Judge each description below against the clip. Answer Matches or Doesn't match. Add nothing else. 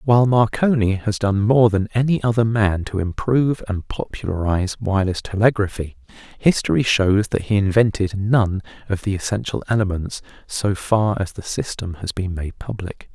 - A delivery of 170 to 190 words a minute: Doesn't match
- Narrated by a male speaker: Matches